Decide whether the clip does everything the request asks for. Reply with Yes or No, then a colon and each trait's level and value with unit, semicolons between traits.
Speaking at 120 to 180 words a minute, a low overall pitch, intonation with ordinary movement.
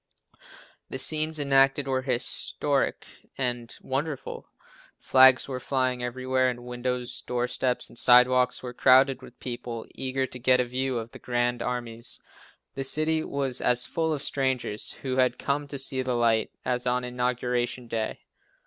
No: average, 150 wpm; low, 125 Hz; narrow, 1.4 semitones